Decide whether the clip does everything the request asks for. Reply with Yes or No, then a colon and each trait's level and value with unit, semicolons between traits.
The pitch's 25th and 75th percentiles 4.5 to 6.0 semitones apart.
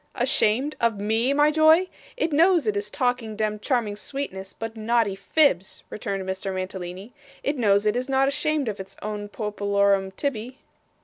Yes: average, 5.2 semitones